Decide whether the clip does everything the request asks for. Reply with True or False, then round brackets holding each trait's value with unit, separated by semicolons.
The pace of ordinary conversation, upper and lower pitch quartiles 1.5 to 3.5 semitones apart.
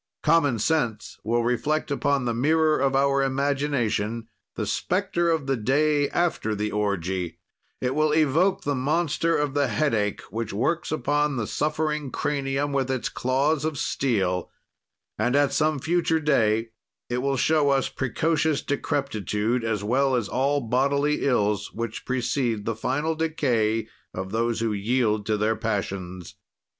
False (150 wpm; 4.8 semitones)